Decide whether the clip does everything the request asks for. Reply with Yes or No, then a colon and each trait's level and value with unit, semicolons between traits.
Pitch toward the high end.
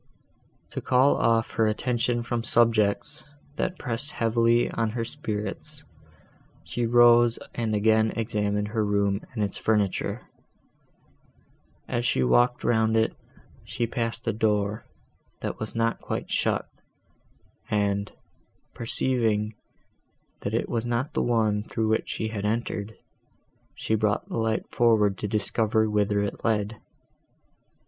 No: low, 110 Hz